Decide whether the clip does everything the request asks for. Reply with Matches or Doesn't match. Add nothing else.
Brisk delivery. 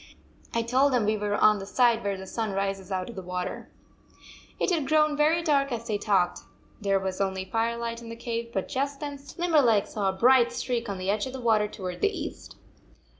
Matches